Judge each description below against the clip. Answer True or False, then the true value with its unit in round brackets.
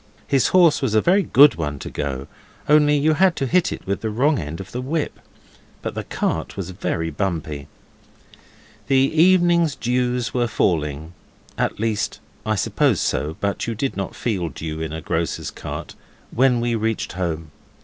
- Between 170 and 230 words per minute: True (175 wpm)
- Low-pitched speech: True (115 Hz)